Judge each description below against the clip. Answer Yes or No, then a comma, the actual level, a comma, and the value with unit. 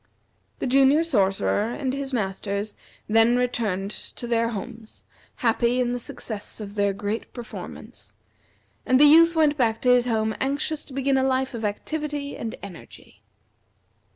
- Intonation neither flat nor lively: Yes, average, 3.9 semitones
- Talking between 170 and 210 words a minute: No, average, 155 wpm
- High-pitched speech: Yes, high, 240 Hz